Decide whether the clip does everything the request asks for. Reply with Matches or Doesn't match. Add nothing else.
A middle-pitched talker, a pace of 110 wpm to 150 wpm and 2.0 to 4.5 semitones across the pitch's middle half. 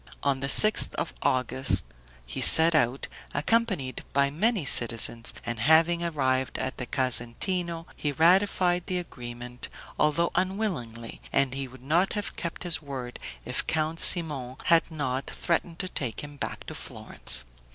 Doesn't match